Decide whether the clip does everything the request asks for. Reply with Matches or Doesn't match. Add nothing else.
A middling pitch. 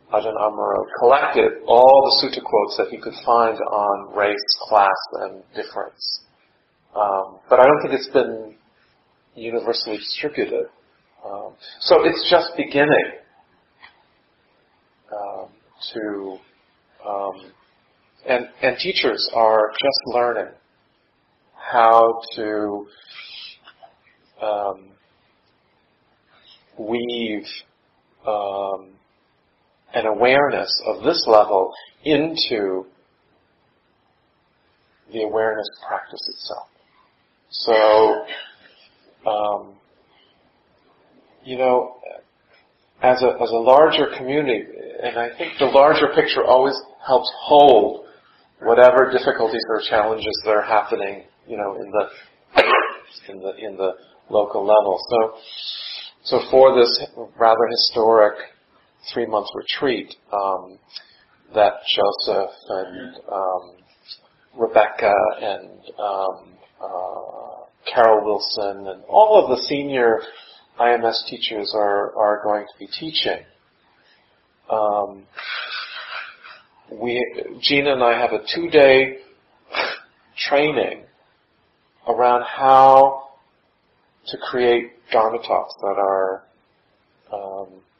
Doesn't match